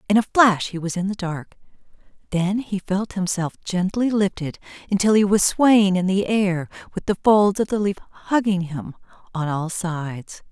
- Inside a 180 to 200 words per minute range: Yes, average, 185 wpm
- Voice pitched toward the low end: No, high, 190 Hz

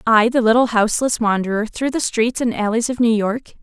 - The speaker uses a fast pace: Yes, fast, 215 wpm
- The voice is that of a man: No, female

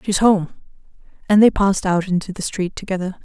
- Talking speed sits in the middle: Yes, average, 185 wpm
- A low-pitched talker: No, high, 190 Hz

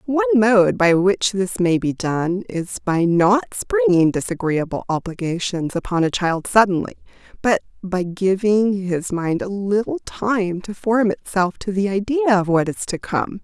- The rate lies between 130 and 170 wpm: Yes, average, 165 wpm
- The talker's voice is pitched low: No, high, 195 Hz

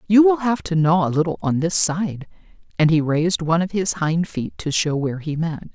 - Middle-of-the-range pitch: Yes, medium, 170 Hz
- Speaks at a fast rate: Yes, fast, 240 wpm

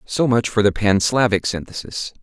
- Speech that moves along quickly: No, average, 190 wpm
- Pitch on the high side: No, low, 110 Hz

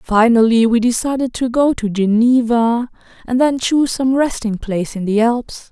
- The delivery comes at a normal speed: Yes, average, 170 wpm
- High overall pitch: Yes, high, 235 Hz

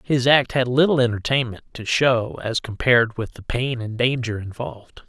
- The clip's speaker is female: No, male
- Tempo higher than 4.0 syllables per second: Yes, 4.9 syllables/s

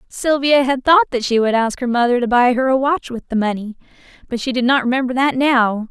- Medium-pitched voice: No, very high, 250 Hz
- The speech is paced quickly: Yes, fast, 245 wpm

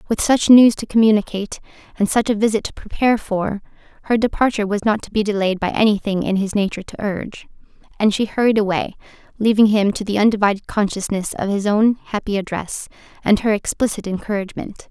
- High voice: Yes, high, 210 Hz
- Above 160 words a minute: Yes, average, 180 wpm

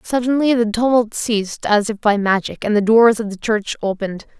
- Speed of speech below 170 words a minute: No, fast, 205 wpm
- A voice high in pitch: Yes, high, 220 Hz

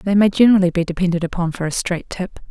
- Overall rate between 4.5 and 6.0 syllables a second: No, 6.9 syllables/s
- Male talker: No, female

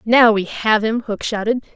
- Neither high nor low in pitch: No, high, 220 Hz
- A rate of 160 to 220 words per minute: Yes, fast, 205 wpm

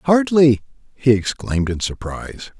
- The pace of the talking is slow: Yes, slow, 115 wpm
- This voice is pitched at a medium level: No, low, 125 Hz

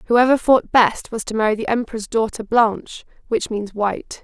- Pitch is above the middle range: Yes, high, 220 Hz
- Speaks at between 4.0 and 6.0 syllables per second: Yes, 5.1 syllables/s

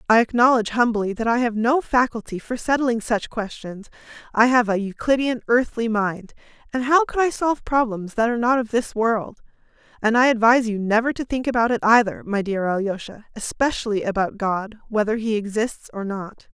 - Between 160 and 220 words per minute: Yes, average, 185 wpm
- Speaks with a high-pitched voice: Yes, high, 230 Hz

